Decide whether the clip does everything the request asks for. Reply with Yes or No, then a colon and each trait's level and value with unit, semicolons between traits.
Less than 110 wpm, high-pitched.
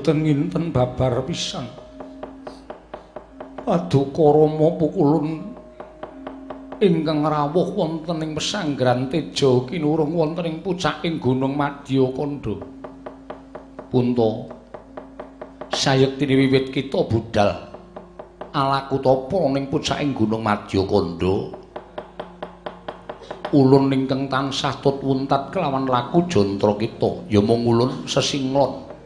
No: average, 90 wpm; medium, 140 Hz